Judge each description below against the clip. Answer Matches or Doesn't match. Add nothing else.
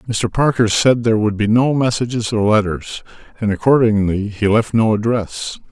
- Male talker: Matches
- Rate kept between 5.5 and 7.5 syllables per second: Doesn't match